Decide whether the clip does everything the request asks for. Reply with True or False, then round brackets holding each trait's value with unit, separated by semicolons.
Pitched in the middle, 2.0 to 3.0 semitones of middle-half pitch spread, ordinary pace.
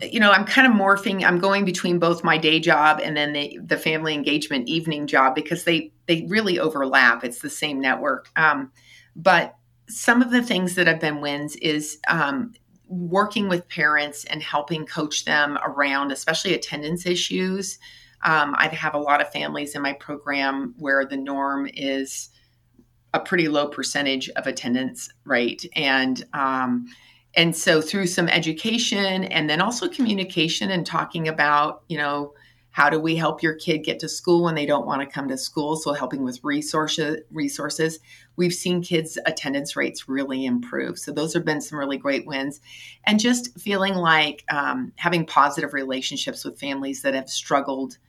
False (150 Hz; 3.8 semitones; 175 wpm)